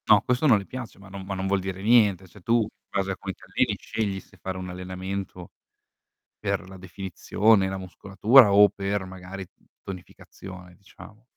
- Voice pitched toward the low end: Yes, very low, 95 Hz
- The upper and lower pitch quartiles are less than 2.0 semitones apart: Yes, narrow, 1.6 semitones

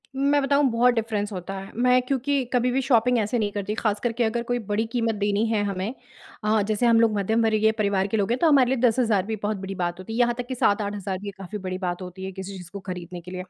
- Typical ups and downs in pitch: Yes, average, 3.6 semitones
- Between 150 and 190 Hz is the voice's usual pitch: No, high, 215 Hz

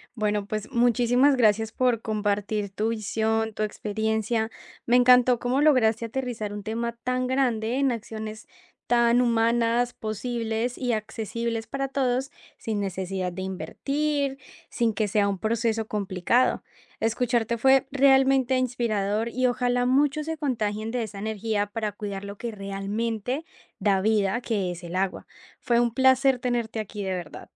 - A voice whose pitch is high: Yes, high, 225 Hz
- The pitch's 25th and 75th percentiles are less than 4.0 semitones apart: Yes, average, 2.9 semitones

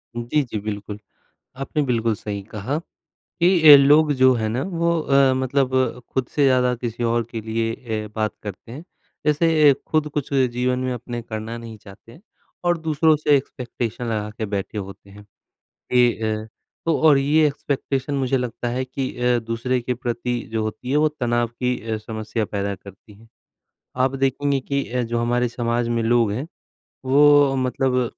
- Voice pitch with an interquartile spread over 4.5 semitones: No, average, 3.3 semitones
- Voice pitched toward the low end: Yes, low, 125 Hz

